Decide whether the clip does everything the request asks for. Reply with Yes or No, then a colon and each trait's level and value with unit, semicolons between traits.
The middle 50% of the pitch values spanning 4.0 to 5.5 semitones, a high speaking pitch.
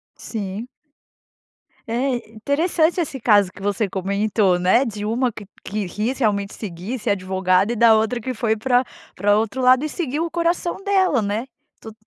Yes: average, 4.3 semitones; high, 220 Hz